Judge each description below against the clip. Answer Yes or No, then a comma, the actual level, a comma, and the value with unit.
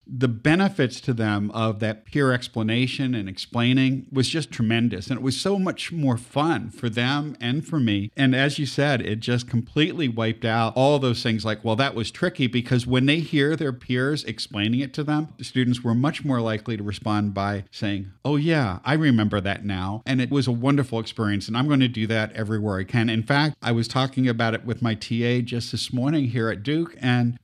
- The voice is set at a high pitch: No, low, 125 Hz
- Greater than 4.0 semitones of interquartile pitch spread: No, average, 3.7 semitones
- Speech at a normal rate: No, fast, 220 wpm